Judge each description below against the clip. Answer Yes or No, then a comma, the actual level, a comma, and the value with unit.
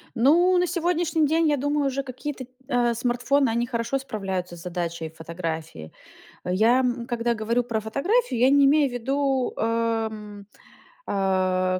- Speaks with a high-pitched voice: Yes, high, 240 Hz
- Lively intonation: Yes, wide, 6.1 semitones